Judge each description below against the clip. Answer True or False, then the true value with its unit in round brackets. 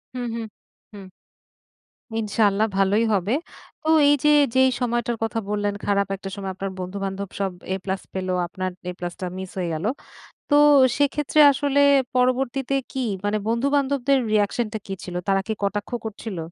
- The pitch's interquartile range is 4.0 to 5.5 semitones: True (4.4 semitones)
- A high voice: True (210 Hz)